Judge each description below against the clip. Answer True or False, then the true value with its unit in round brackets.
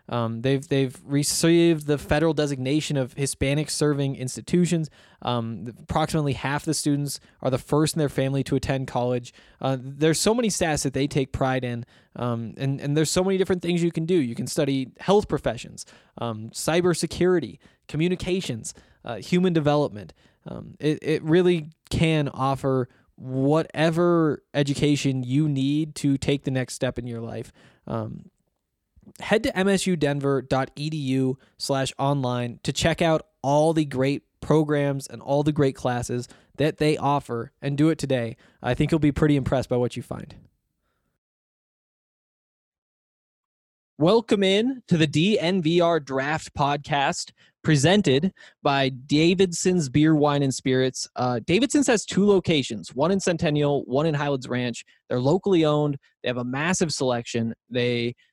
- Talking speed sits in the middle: True (150 wpm)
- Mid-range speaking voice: True (145 Hz)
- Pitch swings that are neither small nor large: True (3.8 semitones)